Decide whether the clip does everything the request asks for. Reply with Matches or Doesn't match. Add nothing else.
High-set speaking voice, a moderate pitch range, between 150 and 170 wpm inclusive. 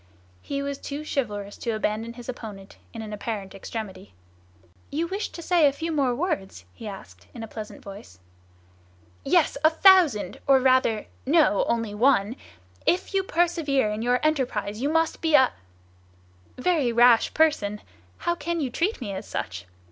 Doesn't match